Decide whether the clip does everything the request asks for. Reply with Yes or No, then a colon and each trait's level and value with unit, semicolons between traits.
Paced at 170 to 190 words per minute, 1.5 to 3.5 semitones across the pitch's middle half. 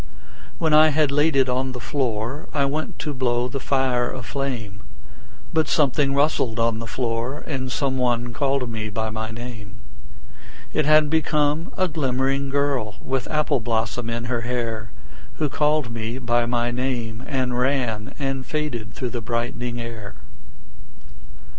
No: average, 155 wpm; average, 3.2 semitones